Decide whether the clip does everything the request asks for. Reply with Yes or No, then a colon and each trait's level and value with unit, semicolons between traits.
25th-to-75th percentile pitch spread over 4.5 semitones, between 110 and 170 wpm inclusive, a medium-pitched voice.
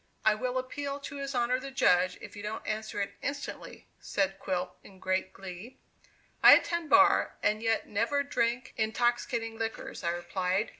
No: average, 4.9 semitones; average, 165 wpm; high, 225 Hz